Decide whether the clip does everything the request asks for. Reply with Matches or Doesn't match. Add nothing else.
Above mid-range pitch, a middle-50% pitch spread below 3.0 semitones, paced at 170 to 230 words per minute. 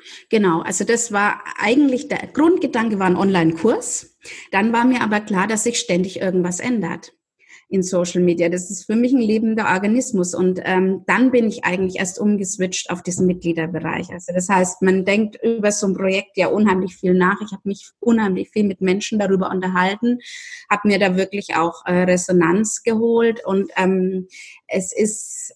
Doesn't match